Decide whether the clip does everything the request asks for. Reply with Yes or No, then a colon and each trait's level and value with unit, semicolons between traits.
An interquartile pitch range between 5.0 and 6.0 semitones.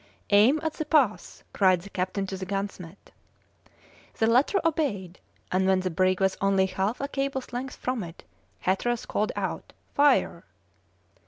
Yes: wide, 5.6 semitones